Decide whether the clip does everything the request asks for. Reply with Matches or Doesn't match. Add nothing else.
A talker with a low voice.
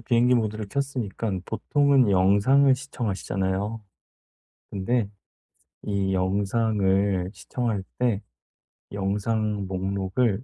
Matches